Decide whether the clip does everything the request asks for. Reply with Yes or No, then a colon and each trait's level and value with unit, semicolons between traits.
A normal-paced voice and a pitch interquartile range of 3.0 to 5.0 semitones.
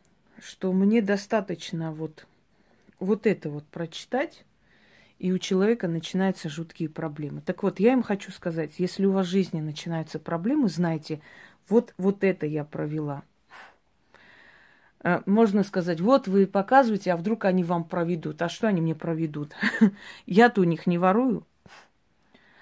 Yes: average, 140 wpm; average, 3.7 semitones